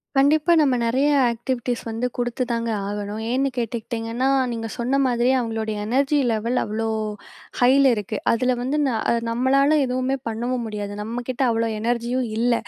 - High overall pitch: Yes, high, 240 Hz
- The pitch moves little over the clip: Yes, narrow, 2.3 semitones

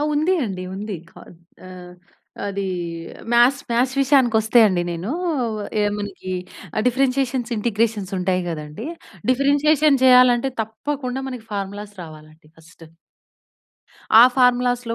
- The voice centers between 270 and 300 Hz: No, high, 230 Hz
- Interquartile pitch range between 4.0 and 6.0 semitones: Yes, average, 4.9 semitones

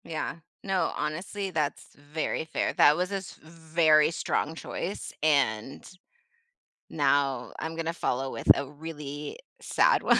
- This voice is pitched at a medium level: Yes, medium, 155 Hz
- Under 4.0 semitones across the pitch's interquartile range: Yes, narrow, 2.6 semitones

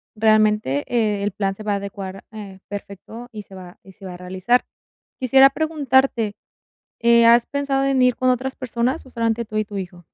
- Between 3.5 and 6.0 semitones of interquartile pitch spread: Yes, average, 4.1 semitones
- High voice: Yes, high, 220 Hz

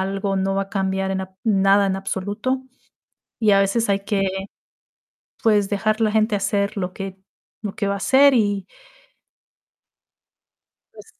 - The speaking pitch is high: Yes, high, 200 Hz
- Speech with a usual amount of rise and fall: No, narrow, 1.7 semitones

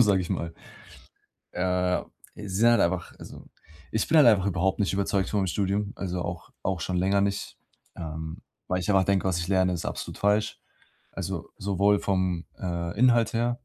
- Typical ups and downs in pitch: No, narrow, 2.1 semitones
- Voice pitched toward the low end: Yes, very low, 95 Hz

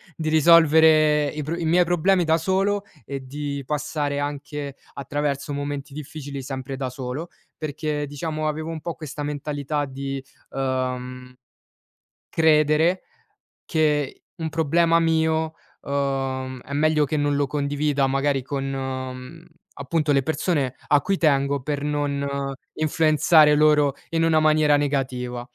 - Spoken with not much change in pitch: Yes, narrow, 2.2 semitones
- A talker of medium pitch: Yes, medium, 145 Hz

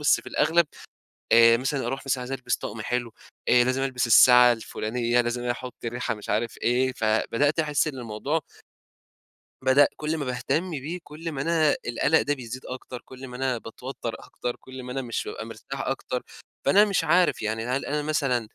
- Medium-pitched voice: No, low, 130 Hz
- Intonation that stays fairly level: No, average, 3.2 semitones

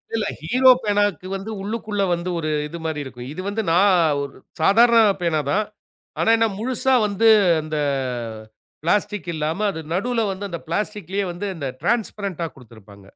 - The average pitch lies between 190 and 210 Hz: Yes, high, 195 Hz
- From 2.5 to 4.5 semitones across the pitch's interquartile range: No, average, 4.9 semitones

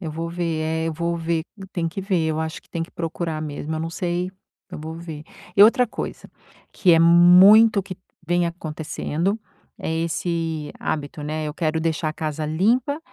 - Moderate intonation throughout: No, narrow, 1.9 semitones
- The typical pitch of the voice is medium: Yes, medium, 165 Hz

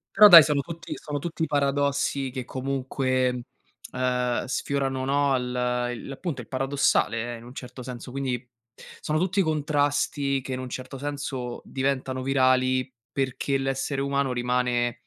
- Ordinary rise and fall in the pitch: No, narrow, 2.0 semitones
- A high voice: No, low, 135 Hz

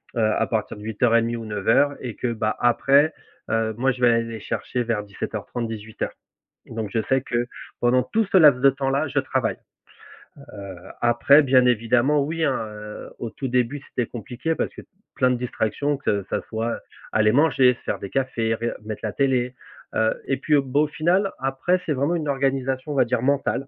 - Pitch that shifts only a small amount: No, average, 3.5 semitones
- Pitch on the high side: No, low, 125 Hz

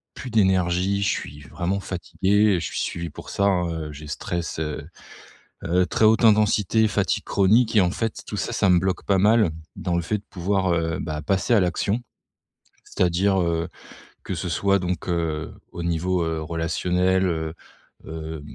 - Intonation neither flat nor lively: Yes, average, 3.2 semitones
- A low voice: Yes, very low, 90 Hz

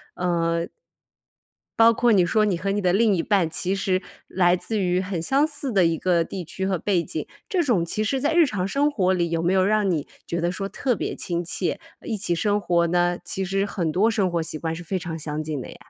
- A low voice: No, medium, 185 Hz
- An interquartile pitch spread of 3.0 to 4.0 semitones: Yes, average, 3.5 semitones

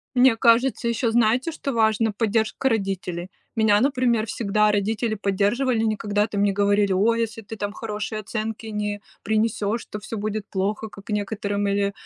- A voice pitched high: Yes, high, 215 Hz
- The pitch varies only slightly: Yes, narrow, 1.9 semitones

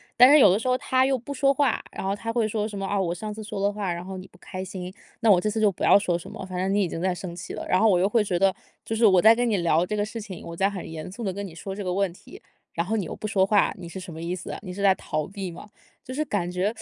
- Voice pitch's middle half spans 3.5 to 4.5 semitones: No, average, 3.0 semitones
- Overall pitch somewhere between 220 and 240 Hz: No, high, 195 Hz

